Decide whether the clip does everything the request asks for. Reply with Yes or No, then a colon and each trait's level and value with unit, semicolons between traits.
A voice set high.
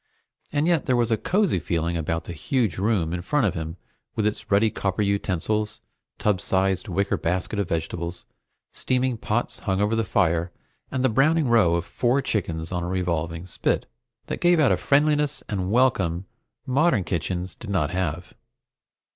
No: low, 100 Hz